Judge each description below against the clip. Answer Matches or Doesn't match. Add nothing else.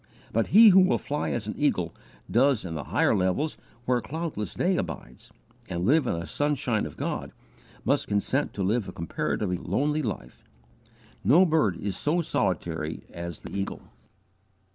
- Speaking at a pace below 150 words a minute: Doesn't match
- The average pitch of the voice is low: Matches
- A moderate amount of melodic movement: Doesn't match